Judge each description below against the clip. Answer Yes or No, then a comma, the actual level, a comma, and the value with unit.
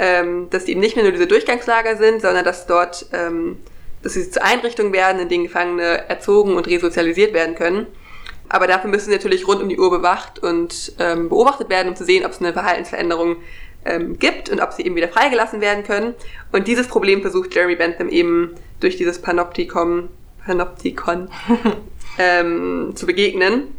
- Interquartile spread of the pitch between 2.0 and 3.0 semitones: No, average, 5.1 semitones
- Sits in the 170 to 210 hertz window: Yes, medium, 185 Hz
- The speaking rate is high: No, average, 170 wpm